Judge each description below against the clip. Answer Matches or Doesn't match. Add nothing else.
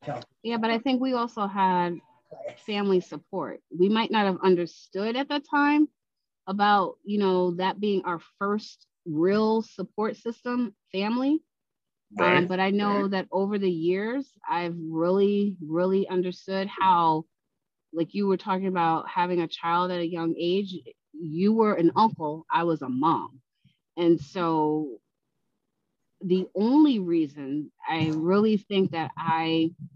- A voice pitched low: Doesn't match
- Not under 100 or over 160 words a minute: Matches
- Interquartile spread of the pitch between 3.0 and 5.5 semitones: Matches